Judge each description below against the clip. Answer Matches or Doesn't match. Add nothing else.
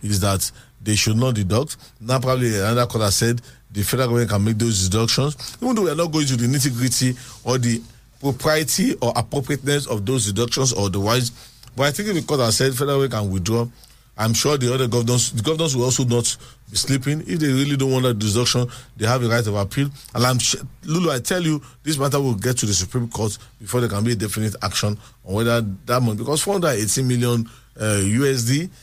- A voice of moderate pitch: Doesn't match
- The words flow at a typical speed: Doesn't match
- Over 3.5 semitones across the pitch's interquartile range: Doesn't match